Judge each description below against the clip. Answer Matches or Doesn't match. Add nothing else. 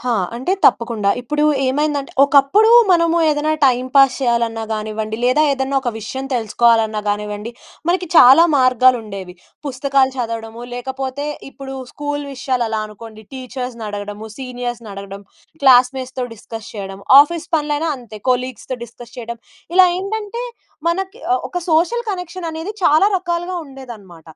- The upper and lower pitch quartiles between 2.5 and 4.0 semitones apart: Doesn't match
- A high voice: Matches